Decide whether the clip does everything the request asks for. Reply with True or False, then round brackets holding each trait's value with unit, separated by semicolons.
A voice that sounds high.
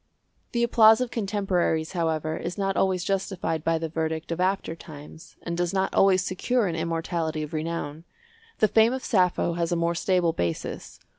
False (170 Hz)